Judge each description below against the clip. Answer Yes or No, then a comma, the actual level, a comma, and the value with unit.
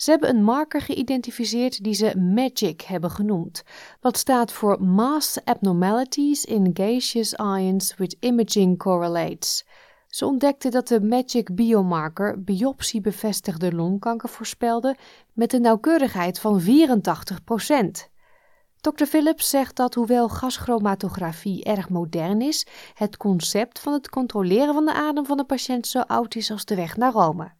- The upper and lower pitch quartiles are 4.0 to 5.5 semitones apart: Yes, average, 4.9 semitones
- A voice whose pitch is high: Yes, high, 225 Hz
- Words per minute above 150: No, slow, 135 wpm